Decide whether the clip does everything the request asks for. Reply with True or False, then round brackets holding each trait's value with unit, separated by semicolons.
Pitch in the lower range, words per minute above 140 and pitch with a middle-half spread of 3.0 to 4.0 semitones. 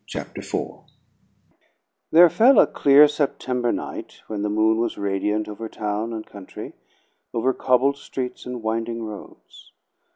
False (115 Hz; 135 wpm; 3.6 semitones)